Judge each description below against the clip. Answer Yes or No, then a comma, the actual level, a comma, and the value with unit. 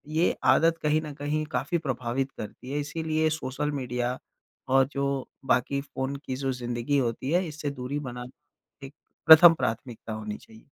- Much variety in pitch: No, average, 3.6 semitones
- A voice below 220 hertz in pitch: Yes, medium, 140 Hz